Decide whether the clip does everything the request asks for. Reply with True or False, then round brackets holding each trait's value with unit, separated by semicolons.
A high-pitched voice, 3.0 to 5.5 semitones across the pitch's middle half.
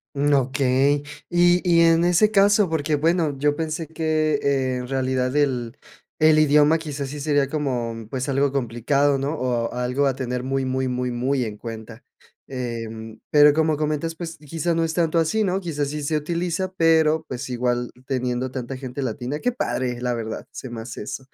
False (140 Hz; 3.9 semitones)